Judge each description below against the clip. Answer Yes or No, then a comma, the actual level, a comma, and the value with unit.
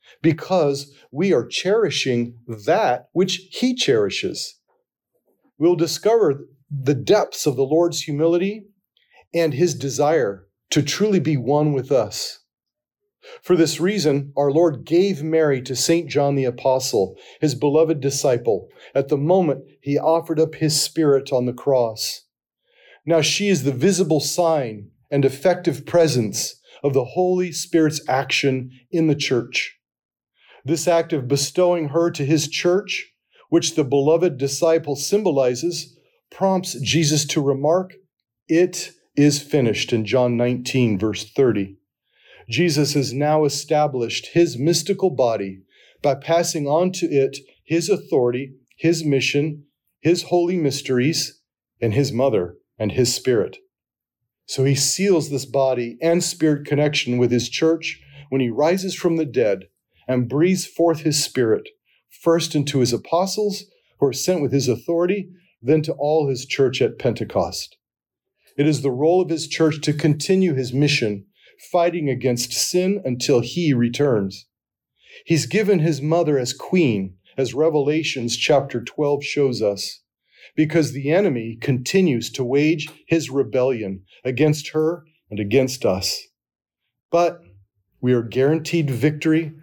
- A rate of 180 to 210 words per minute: No, slow, 135 wpm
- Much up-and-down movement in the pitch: No, average, 4.3 semitones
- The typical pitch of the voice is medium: Yes, medium, 150 Hz